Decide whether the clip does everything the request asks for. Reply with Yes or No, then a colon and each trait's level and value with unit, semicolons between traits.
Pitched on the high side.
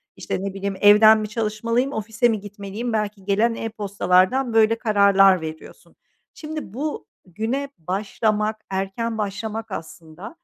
Yes: high, 210 Hz